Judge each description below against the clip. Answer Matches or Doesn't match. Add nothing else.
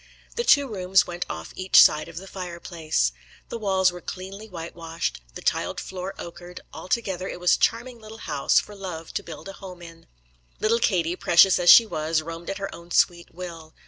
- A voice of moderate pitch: Matches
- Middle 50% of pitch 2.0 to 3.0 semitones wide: Matches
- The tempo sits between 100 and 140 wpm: Doesn't match